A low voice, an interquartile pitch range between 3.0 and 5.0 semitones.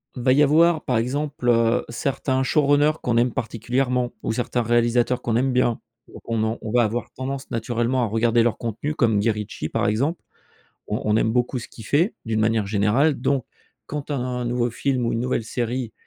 No: low, 120 Hz; narrow, 2.6 semitones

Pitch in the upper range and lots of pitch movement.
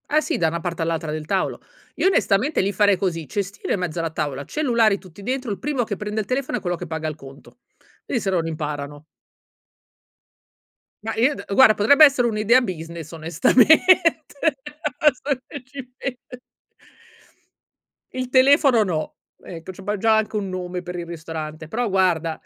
Yes: high, 195 Hz; wide, 7.2 semitones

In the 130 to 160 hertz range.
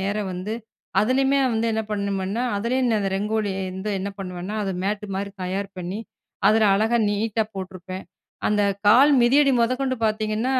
No: high, 210 Hz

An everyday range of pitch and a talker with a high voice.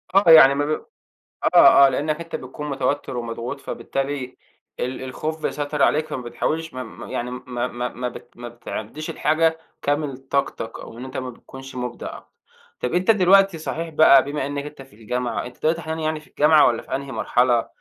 No: average, 3.7 semitones; medium, 140 Hz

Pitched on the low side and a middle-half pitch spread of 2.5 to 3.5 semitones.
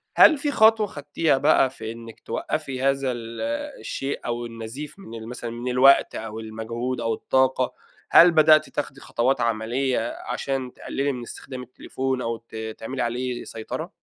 Yes: low, 125 Hz; average, 2.9 semitones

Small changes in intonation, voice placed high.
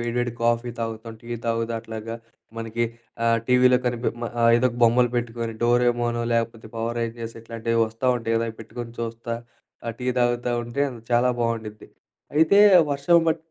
No: narrow, 1.0 semitones; low, 115 Hz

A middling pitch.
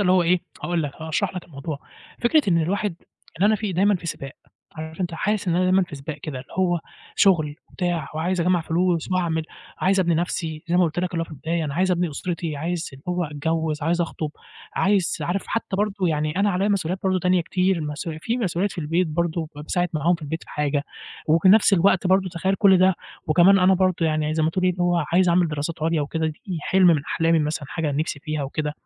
Yes: medium, 170 Hz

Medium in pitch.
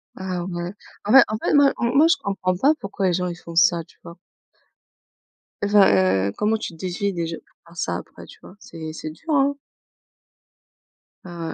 Yes: medium, 180 Hz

